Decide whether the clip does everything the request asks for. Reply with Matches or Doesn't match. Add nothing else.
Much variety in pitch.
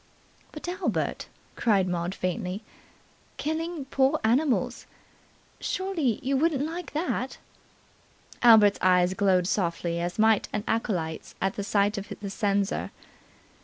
Matches